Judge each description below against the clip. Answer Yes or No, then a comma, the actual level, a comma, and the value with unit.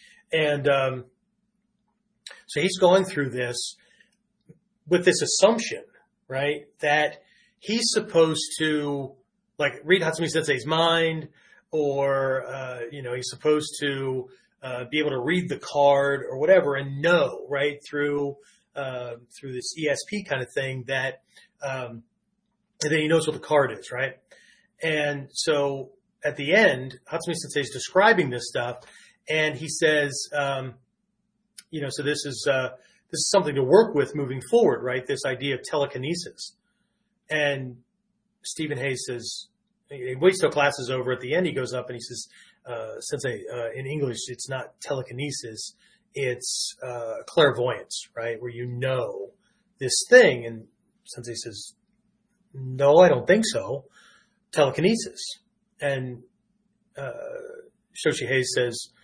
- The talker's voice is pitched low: No, medium, 145 Hz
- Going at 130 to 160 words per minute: Yes, average, 145 wpm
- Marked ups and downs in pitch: Yes, wide, 6.7 semitones